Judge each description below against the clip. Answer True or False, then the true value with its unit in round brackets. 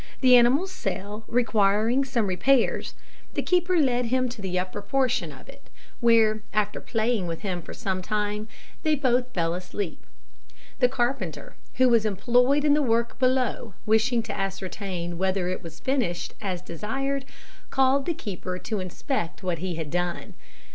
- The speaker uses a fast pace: False (160 wpm)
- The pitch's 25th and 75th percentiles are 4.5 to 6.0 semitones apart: True (5.3 semitones)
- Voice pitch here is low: False (220 Hz)